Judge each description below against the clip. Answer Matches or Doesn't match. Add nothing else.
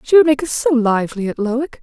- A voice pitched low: Doesn't match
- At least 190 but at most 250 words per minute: Doesn't match